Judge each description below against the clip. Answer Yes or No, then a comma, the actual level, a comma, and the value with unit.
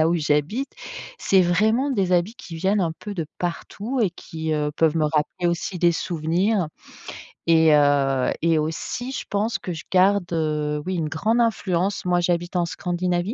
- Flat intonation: No, average, 3.7 semitones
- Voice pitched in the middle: Yes, medium, 175 Hz